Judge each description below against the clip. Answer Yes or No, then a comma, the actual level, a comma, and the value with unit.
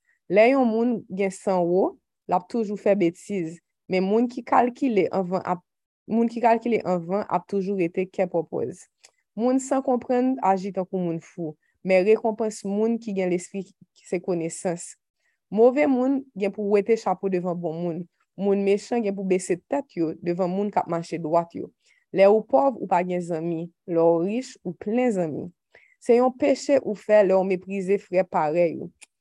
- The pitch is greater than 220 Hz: No, high, 195 Hz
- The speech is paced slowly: No, average, 175 wpm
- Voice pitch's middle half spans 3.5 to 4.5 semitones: Yes, average, 4.2 semitones